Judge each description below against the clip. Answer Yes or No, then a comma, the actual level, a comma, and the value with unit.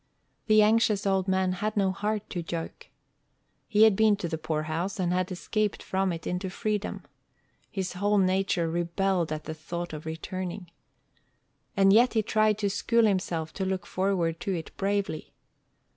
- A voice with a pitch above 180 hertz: Yes, high, 190 Hz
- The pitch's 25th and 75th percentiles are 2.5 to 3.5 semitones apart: Yes, average, 3.2 semitones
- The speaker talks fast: No, average, 165 wpm